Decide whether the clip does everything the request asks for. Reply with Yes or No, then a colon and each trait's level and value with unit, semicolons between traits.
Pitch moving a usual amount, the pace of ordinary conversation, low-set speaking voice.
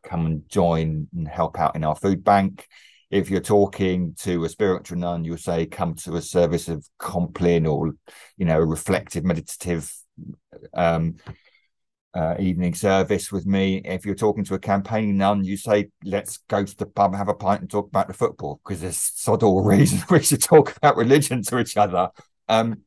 Yes: average, 3.0 semitones; average, 190 wpm; very low, 95 Hz